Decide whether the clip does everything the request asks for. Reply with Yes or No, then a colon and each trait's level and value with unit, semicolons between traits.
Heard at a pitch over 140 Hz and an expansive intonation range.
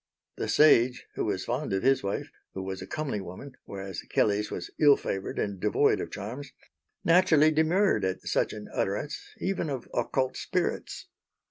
No: low, 125 Hz; wide, 7.4 semitones